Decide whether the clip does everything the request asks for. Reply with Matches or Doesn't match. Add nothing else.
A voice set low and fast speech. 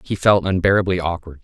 Doesn't match